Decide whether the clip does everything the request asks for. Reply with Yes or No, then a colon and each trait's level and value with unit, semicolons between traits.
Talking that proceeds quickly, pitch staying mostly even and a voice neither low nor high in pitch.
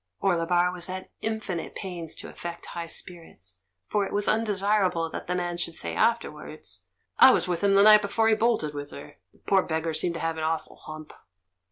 No: fast, 220 wpm; average, 3.5 semitones; medium, 175 Hz